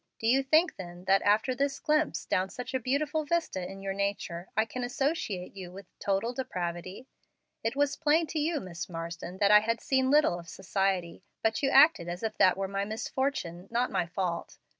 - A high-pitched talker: Yes, high, 210 Hz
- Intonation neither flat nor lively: No, wide, 6.7 semitones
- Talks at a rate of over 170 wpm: Yes, average, 200 wpm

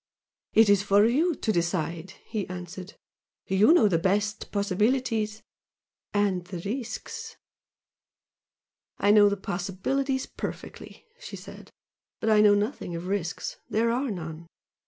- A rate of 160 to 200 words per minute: No, slow, 135 wpm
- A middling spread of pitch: Yes, average, 3.6 semitones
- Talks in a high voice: Yes, high, 205 Hz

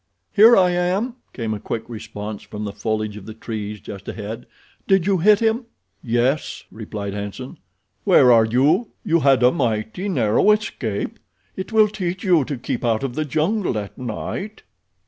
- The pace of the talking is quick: No, average, 170 wpm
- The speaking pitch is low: Yes, low, 125 Hz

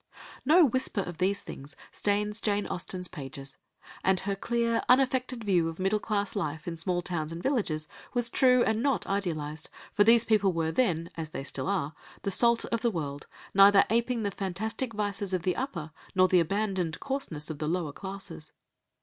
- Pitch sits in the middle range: No, high, 195 Hz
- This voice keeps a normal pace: Yes, average, 185 wpm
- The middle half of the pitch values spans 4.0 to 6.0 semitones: Yes, wide, 5.4 semitones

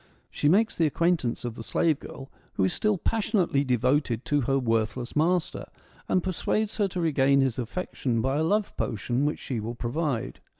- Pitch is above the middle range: No, medium, 140 Hz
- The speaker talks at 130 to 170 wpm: No, average, 180 wpm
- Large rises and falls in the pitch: Yes, wide, 6.2 semitones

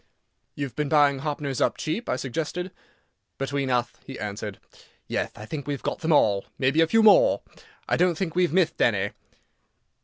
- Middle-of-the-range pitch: Yes, medium, 145 Hz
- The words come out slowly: No, average, 175 wpm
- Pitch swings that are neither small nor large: Yes, average, 4.4 semitones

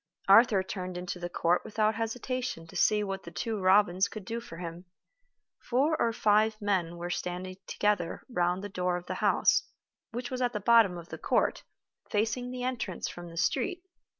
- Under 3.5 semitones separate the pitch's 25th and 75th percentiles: No, average, 4.3 semitones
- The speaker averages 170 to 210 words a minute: Yes, average, 185 wpm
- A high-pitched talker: Yes, high, 200 Hz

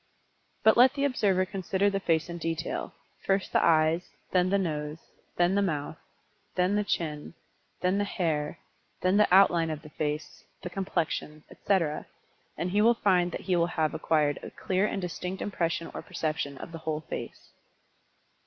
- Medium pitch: Yes, medium, 175 Hz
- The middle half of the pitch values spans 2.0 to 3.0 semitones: No, average, 3.6 semitones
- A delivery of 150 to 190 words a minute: Yes, average, 170 wpm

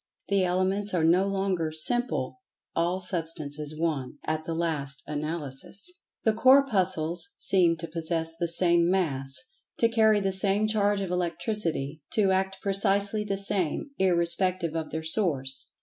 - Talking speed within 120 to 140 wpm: Yes, slow, 135 wpm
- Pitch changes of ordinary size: Yes, average, 3.7 semitones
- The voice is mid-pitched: Yes, medium, 180 Hz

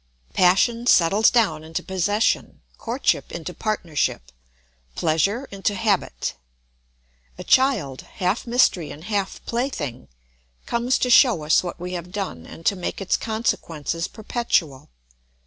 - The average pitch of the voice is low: No, high, 190 Hz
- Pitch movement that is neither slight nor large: No, wide, 5.7 semitones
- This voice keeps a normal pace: No, slow, 125 wpm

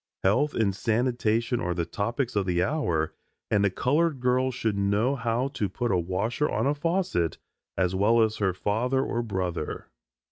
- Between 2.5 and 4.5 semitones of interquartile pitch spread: No, average, 5.0 semitones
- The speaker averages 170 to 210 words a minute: Yes, average, 175 wpm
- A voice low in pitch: Yes, low, 110 Hz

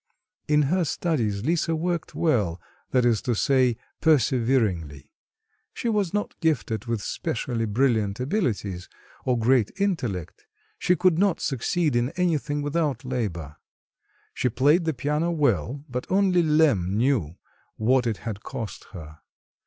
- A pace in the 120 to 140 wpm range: Yes, slow, 135 wpm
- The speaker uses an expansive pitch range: Yes, wide, 6.5 semitones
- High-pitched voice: No, low, 130 Hz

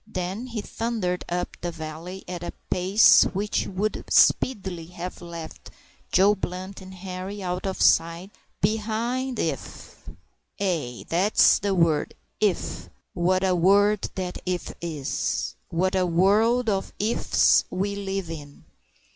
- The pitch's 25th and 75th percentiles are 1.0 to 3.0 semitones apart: Yes, average, 2.7 semitones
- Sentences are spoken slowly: Yes, slow, 130 wpm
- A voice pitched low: No, medium, 185 Hz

